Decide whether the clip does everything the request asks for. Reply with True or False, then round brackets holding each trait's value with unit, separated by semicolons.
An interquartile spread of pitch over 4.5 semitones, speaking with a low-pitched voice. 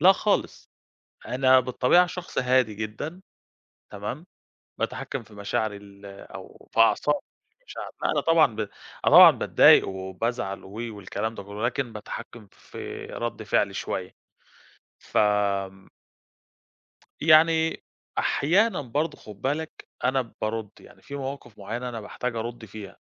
True (5.0 semitones; 115 Hz)